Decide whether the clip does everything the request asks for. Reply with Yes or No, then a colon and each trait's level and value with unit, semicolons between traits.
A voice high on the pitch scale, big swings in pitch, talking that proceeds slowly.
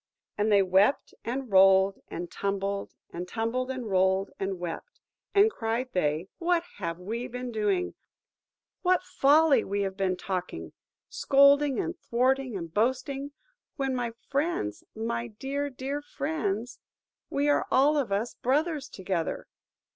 Yes: high, 235 Hz; wide, 6.2 semitones; slow, 130 wpm